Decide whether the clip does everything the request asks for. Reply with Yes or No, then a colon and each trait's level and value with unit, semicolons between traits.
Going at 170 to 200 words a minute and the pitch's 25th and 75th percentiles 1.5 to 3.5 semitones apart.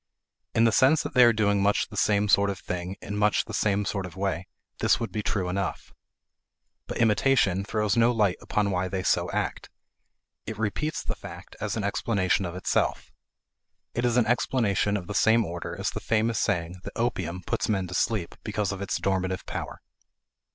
Yes: average, 195 wpm; average, 2.8 semitones